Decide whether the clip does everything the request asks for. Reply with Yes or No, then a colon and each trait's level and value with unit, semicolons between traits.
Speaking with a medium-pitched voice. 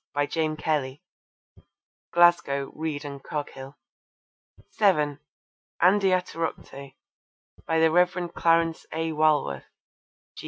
Yes: medium, 155 Hz